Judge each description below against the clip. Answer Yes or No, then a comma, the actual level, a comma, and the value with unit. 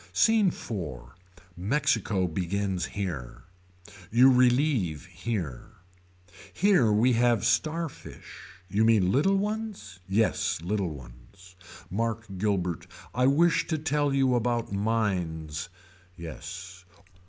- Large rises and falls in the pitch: Yes, wide, 6.2 semitones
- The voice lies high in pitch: No, low, 105 Hz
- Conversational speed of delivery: No, slow, 105 wpm